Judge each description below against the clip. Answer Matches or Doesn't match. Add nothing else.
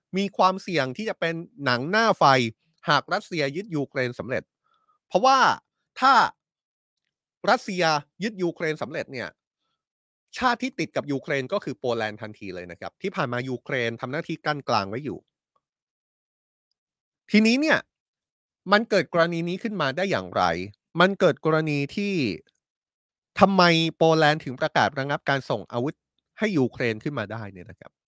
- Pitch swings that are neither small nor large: Doesn't match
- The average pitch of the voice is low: Doesn't match